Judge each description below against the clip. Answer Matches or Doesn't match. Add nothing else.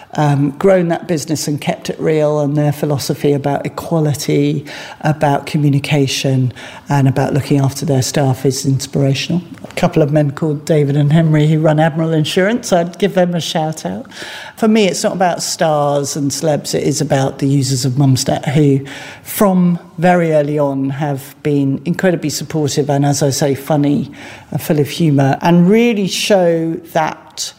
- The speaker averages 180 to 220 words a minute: Doesn't match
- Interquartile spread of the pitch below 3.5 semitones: Matches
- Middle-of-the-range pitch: Matches